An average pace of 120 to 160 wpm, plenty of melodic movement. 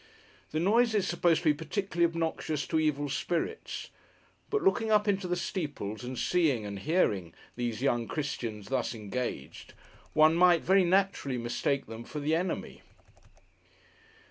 Yes: average, 145 wpm; wide, 6.4 semitones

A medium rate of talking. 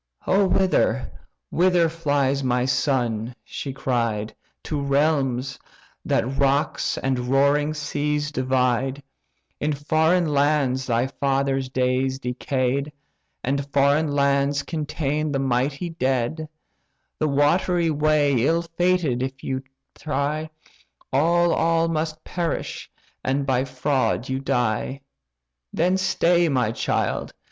No: slow, 110 wpm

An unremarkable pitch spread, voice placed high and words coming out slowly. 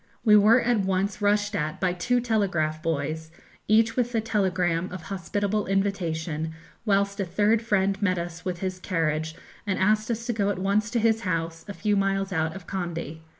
No: average, 3.7 semitones; high, 195 Hz; average, 190 wpm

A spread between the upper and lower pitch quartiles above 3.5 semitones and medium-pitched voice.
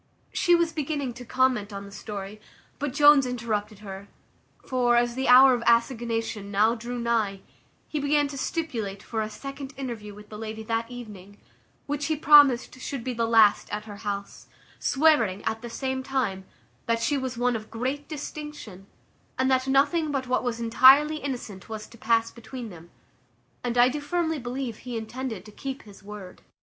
No: average, 3.9 semitones; high, 240 Hz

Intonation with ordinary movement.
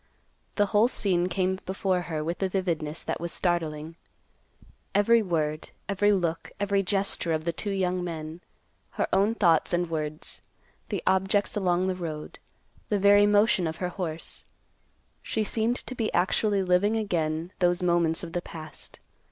Yes: average, 3.3 semitones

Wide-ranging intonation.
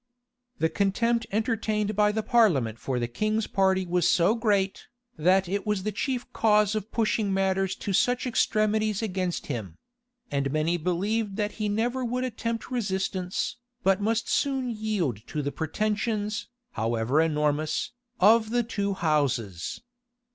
No: average, 4.4 semitones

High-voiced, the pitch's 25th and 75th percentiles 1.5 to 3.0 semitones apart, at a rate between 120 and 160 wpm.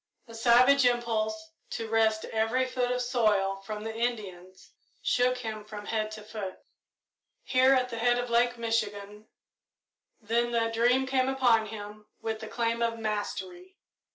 Yes: high, 230 Hz; narrow, 2.4 semitones; average, 155 wpm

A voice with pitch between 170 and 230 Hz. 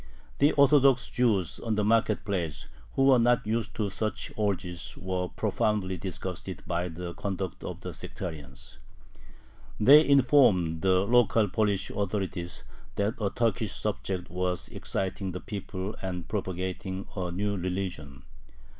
No: very low, 95 Hz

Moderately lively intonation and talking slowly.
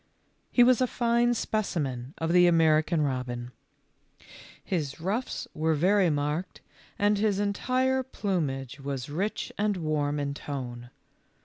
No: wide, 6.5 semitones; slow, 125 wpm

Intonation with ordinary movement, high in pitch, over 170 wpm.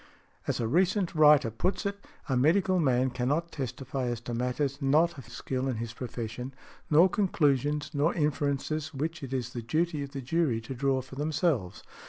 No: average, 3.9 semitones; medium, 140 Hz; average, 180 wpm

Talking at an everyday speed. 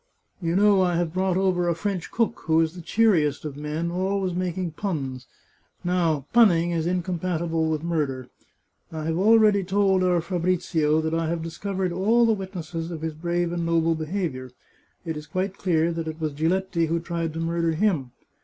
Yes: average, 180 wpm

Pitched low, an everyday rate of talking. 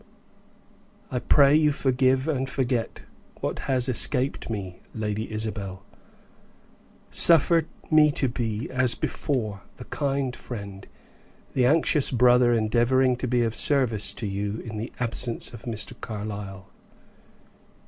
No: low, 120 Hz; slow, 125 wpm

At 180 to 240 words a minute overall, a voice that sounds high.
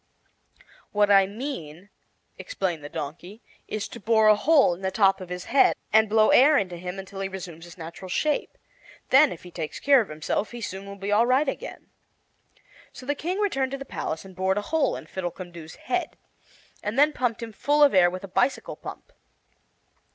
Yes: average, 200 wpm; high, 200 Hz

